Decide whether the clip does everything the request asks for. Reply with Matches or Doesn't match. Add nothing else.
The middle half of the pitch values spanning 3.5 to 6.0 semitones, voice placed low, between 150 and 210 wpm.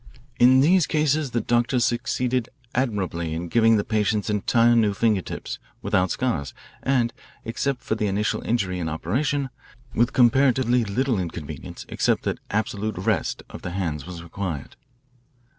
Doesn't match